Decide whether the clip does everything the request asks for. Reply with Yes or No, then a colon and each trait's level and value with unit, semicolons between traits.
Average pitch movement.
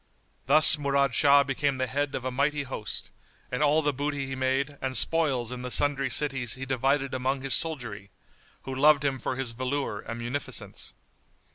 No: narrow, 2.0 semitones